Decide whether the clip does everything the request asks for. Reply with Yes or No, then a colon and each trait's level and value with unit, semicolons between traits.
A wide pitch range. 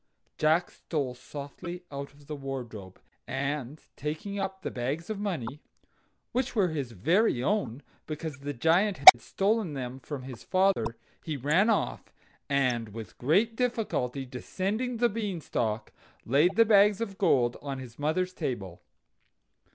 Yes: wide, 7.2 semitones